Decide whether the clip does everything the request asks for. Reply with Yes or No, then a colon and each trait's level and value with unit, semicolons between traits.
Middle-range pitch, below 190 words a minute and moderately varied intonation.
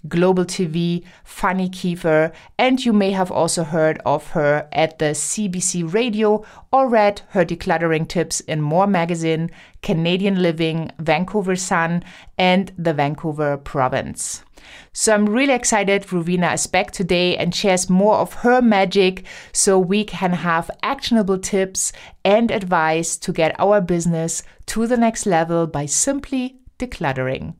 Yes: medium, 180 Hz; average, 140 wpm; average, 3.6 semitones